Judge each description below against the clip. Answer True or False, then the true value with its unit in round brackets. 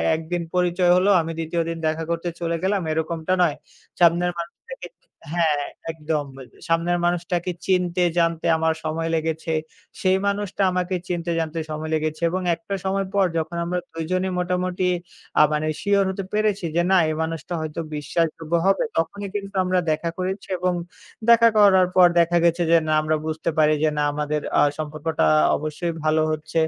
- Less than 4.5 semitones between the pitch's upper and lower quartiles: True (2.5 semitones)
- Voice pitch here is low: False (170 Hz)